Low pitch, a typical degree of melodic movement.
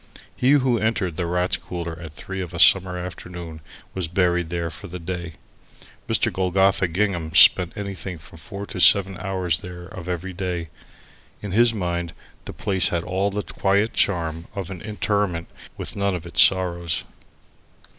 No: very low, 90 Hz; narrow, 2.2 semitones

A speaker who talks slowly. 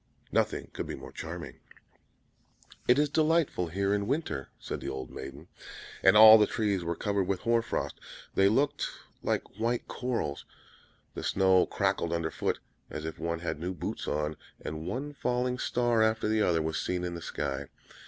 No: average, 175 wpm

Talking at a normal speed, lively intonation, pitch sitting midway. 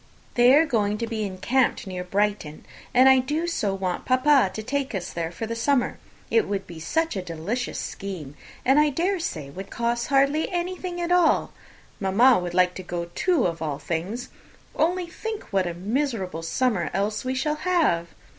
No: average, 190 wpm; wide, 7.7 semitones; high, 230 Hz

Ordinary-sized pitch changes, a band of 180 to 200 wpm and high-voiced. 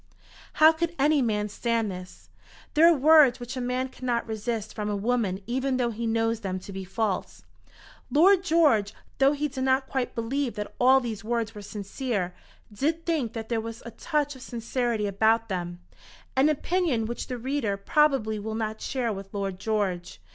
Yes: average, 4.3 semitones; average, 185 wpm; high, 235 Hz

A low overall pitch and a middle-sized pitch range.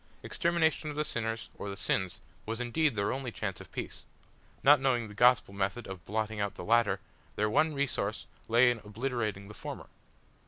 Yes: low, 115 Hz; average, 4.1 semitones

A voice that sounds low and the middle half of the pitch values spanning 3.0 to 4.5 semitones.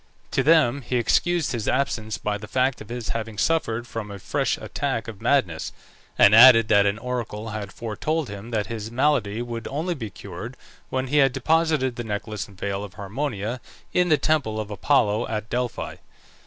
Yes: low, 115 Hz; average, 4.1 semitones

